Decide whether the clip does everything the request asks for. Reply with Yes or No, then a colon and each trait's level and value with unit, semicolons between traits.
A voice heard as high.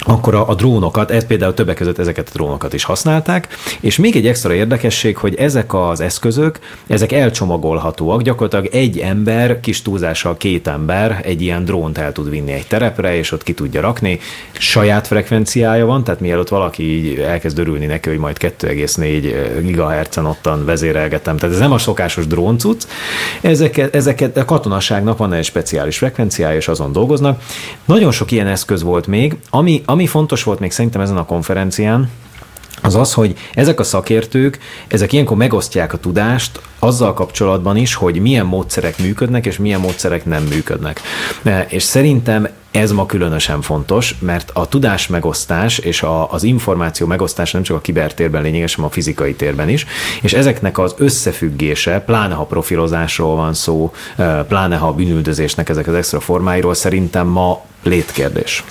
No: very low, 95 Hz